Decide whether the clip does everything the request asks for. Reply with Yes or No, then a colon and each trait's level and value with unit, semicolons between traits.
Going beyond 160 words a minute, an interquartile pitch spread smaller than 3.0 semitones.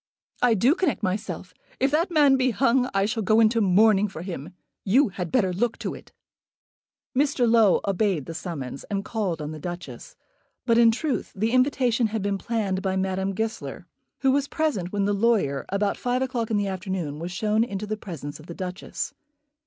No: average, 190 wpm; average, 4.2 semitones